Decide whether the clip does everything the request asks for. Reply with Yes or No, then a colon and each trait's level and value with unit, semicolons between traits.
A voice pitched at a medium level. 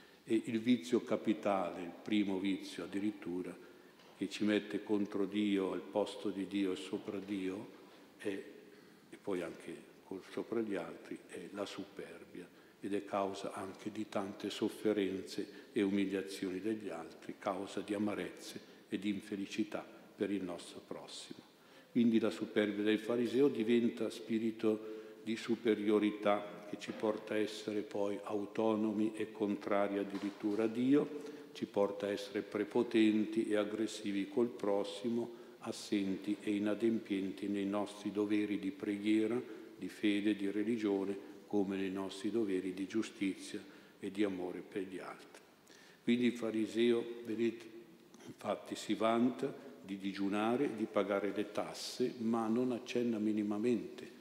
No: low, 105 Hz